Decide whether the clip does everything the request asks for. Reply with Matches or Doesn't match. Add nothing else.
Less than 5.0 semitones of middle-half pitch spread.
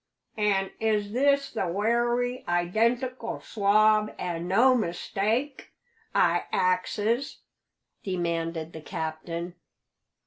Doesn't match